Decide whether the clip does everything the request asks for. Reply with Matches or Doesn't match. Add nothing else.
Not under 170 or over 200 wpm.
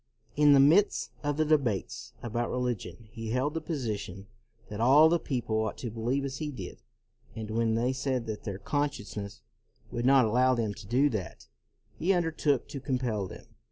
Matches